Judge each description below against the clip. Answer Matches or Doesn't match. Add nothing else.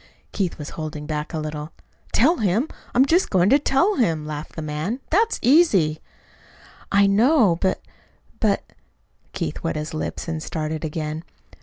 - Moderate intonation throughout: Doesn't match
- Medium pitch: Matches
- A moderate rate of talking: Matches